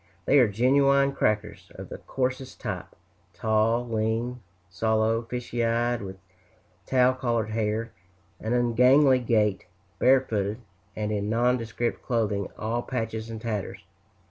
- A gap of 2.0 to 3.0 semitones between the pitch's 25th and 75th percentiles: Yes, narrow, 2.4 semitones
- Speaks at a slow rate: Yes, slow, 120 wpm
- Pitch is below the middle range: Yes, low, 115 Hz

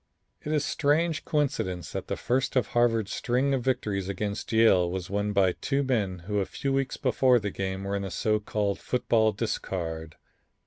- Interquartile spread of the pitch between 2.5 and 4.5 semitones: No, average, 5.0 semitones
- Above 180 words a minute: Yes, average, 190 wpm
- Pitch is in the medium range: No, low, 105 Hz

